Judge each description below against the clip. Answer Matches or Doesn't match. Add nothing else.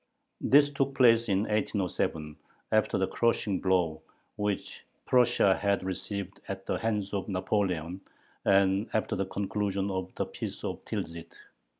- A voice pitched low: Matches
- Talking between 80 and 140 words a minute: Matches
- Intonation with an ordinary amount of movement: Doesn't match